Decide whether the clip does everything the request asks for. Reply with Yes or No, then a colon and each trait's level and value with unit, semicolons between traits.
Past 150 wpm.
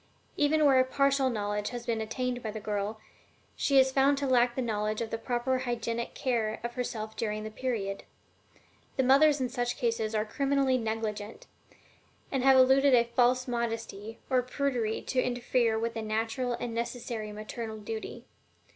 Yes: average, 170 wpm